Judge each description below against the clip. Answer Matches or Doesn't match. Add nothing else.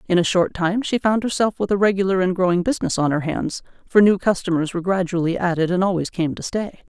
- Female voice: Matches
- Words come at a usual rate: Doesn't match